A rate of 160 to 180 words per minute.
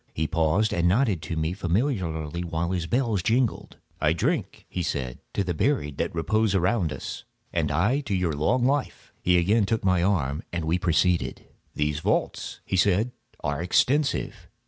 Yes: average, 170 wpm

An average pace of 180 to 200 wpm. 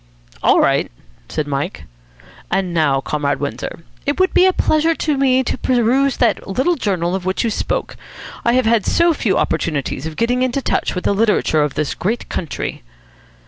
Yes: average, 185 wpm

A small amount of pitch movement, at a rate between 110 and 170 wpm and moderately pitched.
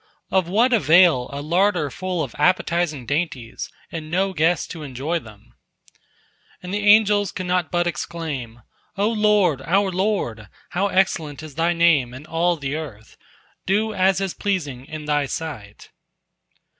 No: average, 4.8 semitones; average, 150 wpm; medium, 170 Hz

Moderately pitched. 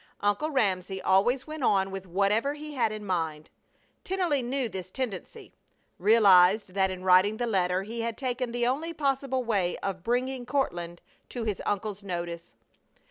No: high, 210 Hz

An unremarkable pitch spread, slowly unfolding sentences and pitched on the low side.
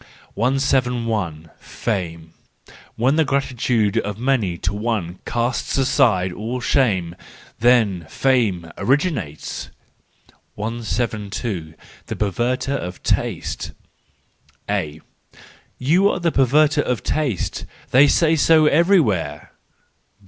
No: wide, 6.3 semitones; slow, 90 wpm; low, 120 Hz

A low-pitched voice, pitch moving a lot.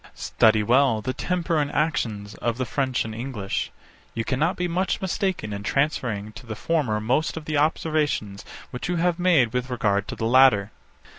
Yes: low, 130 Hz; wide, 6.2 semitones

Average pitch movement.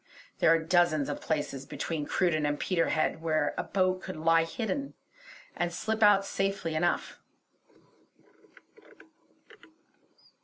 Yes: average, 3.1 semitones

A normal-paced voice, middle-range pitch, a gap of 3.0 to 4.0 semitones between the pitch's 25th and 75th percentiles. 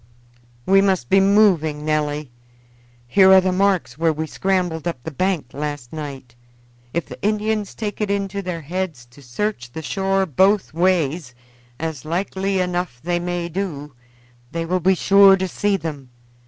No: average, 160 wpm; medium, 175 Hz; average, 4.4 semitones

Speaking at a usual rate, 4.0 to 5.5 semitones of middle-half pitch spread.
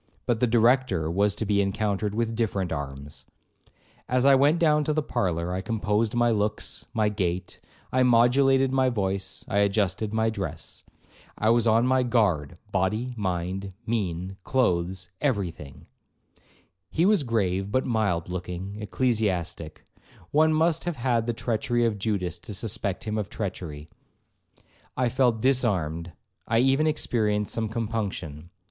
Yes: average, 150 wpm; average, 4.6 semitones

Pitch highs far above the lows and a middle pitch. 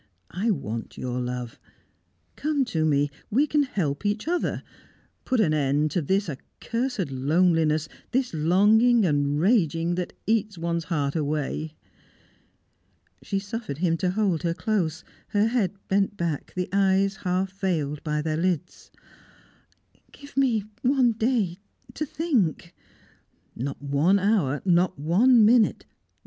Yes: wide, 6.0 semitones; medium, 180 Hz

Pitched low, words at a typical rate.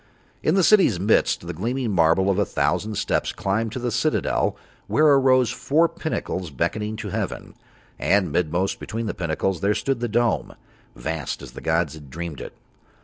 Yes: low, 105 Hz; average, 175 wpm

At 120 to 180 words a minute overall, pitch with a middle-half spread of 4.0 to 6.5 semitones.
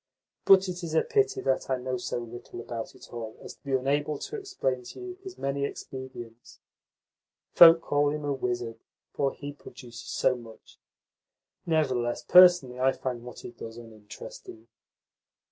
Yes: average, 160 wpm; average, 4.5 semitones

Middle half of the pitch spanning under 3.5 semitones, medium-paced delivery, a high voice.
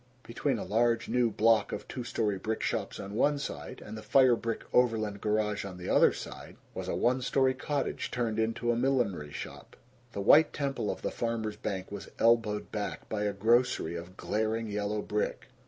No: narrow, 2.6 semitones; average, 190 wpm; low, 110 Hz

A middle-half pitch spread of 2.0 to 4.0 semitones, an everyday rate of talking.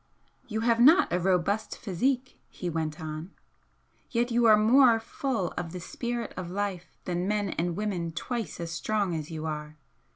No: wide, 5.4 semitones; average, 170 wpm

